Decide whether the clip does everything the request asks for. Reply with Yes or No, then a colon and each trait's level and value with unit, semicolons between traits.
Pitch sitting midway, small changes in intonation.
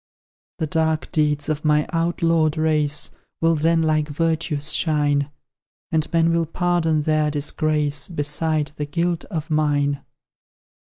Yes: medium, 155 Hz; narrow, 1.7 semitones